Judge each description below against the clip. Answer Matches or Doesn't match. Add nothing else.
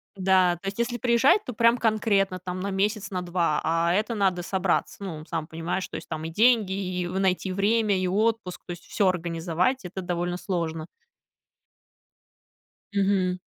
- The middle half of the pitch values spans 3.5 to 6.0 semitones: Doesn't match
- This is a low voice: Doesn't match